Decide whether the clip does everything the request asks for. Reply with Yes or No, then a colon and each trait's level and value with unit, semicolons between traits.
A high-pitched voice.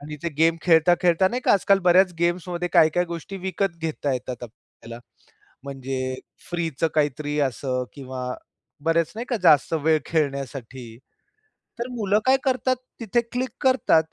No: medium, 165 Hz